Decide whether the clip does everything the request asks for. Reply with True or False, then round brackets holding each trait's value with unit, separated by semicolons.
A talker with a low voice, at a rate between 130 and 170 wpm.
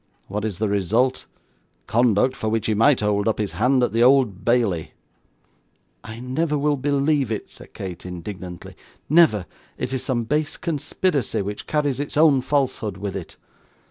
True (120 Hz; 165 wpm)